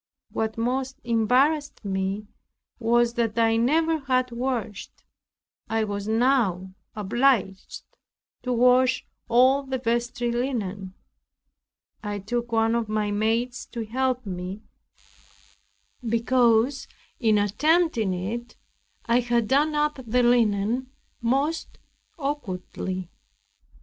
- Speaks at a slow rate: Yes, slow, 105 wpm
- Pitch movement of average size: Yes, average, 3.3 semitones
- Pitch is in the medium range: No, high, 235 Hz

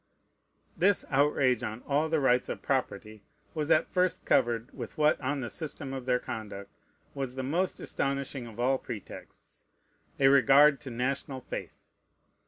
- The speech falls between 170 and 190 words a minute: No, average, 155 wpm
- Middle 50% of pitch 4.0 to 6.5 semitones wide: No, average, 2.9 semitones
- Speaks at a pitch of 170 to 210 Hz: No, low, 135 Hz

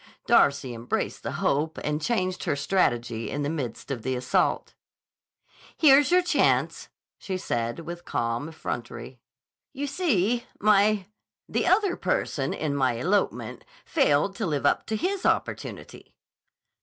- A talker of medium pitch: Yes, medium, 165 Hz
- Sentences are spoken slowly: Yes, slow, 130 wpm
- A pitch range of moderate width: No, wide, 8.9 semitones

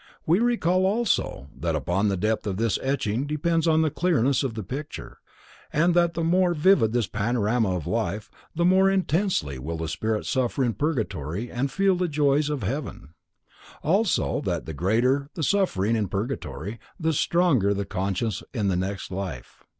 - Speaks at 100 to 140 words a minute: No, average, 170 wpm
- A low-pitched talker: Yes, low, 125 Hz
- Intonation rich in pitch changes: Yes, wide, 8.6 semitones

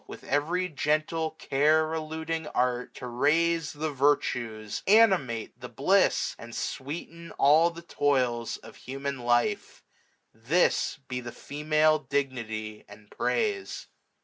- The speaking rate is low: Yes, slow, 120 wpm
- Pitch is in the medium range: Yes, medium, 145 Hz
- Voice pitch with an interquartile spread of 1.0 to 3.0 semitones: No, average, 4.6 semitones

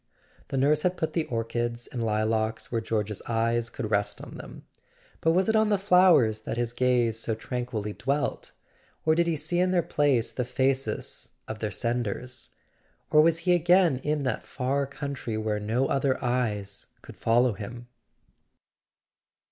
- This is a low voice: Yes, low, 125 Hz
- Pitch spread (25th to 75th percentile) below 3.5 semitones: No, average, 5.1 semitones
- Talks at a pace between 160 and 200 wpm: Yes, average, 170 wpm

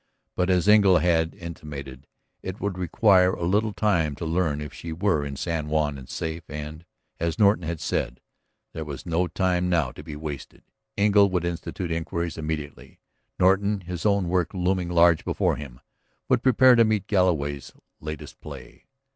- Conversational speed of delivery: Yes, average, 170 wpm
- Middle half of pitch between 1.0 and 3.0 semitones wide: No, average, 3.5 semitones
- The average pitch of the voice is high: No, very low, 85 Hz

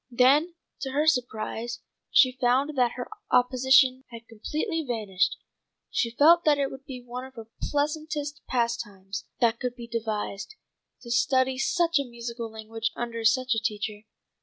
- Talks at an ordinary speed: Yes, average, 155 wpm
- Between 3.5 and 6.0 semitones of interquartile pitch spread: No, average, 3.1 semitones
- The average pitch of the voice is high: Yes, very high, 250 Hz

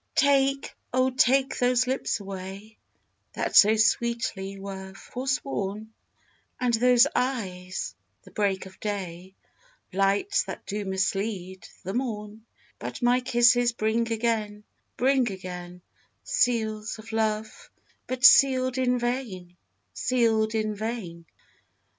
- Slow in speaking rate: Yes, slow, 110 wpm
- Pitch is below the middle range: No, high, 220 Hz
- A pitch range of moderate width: Yes, average, 4.2 semitones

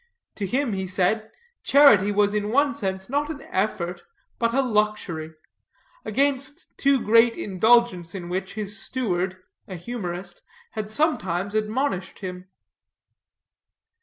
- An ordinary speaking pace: No, slow, 125 wpm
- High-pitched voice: Yes, high, 210 Hz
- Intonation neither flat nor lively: Yes, average, 4.7 semitones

